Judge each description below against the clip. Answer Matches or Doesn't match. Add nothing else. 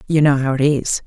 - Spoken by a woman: Matches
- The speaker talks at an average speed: Doesn't match